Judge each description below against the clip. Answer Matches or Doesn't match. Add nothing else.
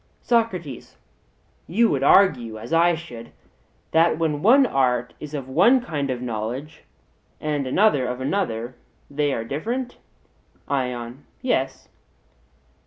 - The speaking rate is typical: Doesn't match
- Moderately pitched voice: Matches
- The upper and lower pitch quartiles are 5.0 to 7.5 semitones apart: Matches